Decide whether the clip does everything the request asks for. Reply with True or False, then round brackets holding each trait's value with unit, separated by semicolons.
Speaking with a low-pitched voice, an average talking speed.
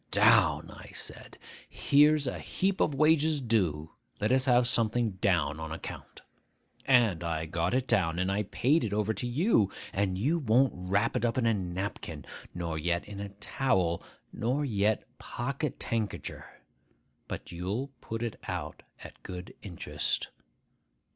True (105 Hz; 150 wpm)